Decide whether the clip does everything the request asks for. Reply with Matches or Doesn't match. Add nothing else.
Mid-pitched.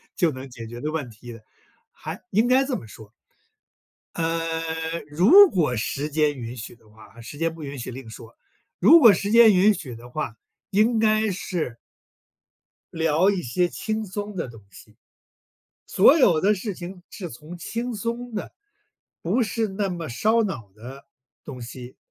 Matches